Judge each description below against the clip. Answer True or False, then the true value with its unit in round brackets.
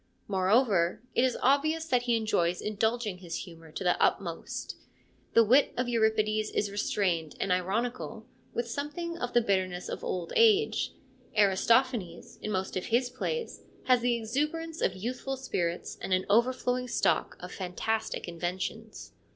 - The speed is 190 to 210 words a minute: False (150 wpm)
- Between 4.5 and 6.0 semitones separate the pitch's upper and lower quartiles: True (5.1 semitones)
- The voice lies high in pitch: True (220 Hz)